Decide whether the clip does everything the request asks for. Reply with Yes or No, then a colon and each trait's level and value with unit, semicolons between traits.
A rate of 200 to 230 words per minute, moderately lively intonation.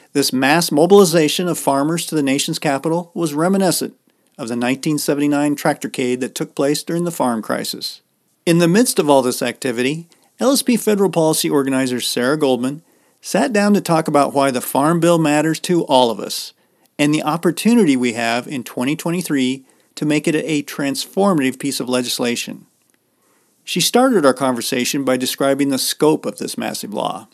No: average, 165 wpm; average, 4.1 semitones